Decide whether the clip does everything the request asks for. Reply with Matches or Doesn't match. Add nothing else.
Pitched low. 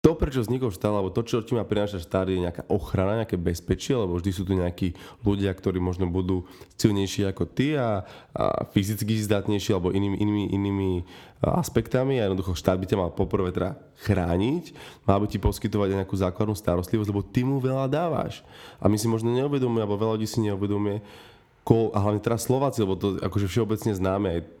Matches